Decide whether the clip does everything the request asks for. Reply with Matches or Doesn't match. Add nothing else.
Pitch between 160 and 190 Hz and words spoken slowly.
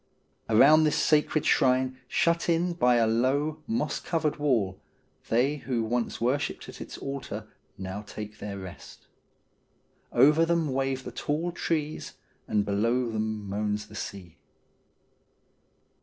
Doesn't match